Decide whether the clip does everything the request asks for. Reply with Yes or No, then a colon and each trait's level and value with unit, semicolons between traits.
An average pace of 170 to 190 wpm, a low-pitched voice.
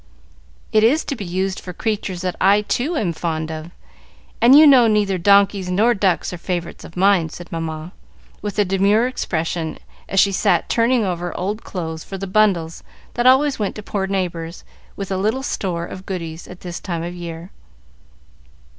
No: average, 185 wpm; high, 190 Hz